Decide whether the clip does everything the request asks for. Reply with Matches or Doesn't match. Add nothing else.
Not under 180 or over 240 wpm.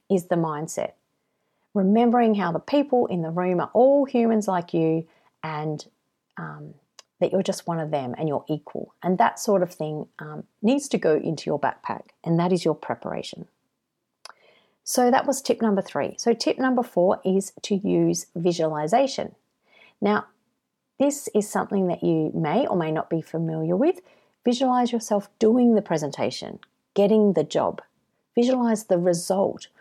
Doesn't match